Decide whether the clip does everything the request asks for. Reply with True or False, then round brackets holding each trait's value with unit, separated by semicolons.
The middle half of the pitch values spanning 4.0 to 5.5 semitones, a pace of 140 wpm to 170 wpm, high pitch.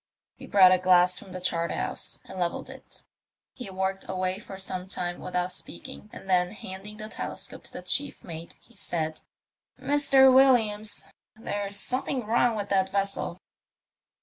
False (3.0 semitones; 160 wpm; 195 Hz)